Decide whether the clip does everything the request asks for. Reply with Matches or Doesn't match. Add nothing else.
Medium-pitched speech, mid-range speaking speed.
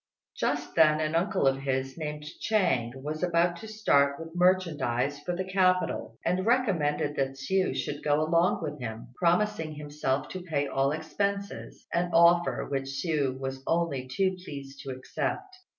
Matches